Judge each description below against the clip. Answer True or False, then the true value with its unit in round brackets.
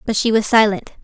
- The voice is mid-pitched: False (215 Hz)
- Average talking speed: False (235 wpm)